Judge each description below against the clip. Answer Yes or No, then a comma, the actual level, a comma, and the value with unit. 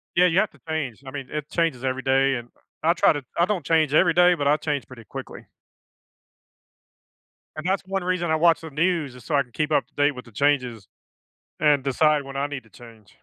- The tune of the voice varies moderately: Yes, average, 3.8 semitones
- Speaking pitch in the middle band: Yes, medium, 145 Hz